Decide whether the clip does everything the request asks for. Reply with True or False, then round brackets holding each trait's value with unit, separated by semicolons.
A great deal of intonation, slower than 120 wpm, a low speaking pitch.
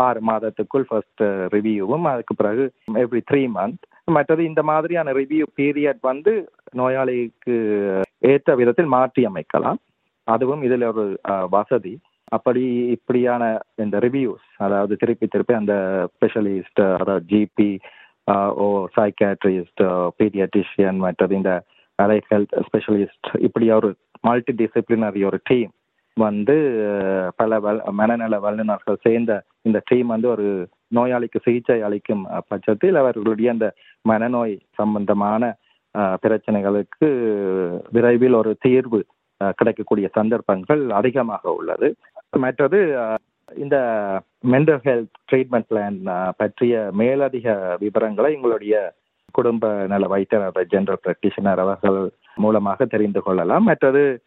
False (3.7 semitones; 105 wpm; 110 Hz)